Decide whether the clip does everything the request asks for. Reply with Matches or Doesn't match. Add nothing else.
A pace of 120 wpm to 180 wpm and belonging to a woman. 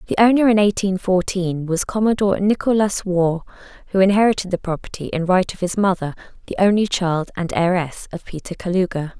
Matches